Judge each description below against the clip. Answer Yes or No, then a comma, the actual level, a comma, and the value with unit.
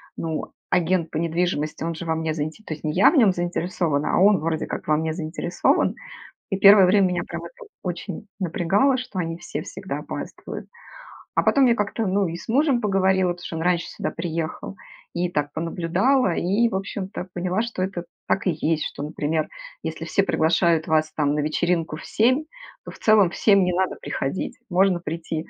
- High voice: No, medium, 175 Hz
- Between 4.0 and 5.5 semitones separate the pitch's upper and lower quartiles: No, average, 3.4 semitones